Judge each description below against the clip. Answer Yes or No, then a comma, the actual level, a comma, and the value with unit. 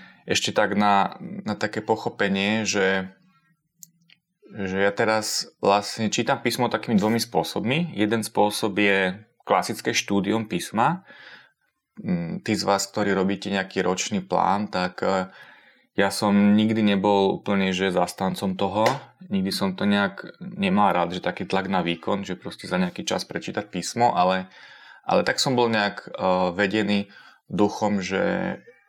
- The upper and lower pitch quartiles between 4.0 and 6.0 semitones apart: No, narrow, 2.6 semitones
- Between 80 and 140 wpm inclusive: Yes, slow, 135 wpm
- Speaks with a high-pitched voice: No, low, 105 Hz